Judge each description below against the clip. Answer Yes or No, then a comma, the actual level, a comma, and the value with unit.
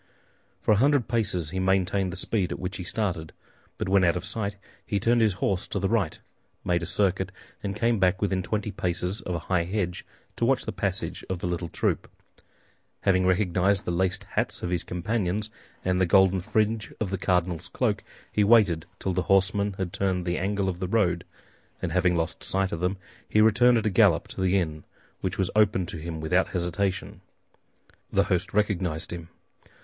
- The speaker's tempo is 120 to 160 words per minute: No, average, 195 wpm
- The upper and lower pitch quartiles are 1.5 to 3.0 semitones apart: Yes, narrow, 2.5 semitones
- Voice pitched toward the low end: Yes, very low, 95 Hz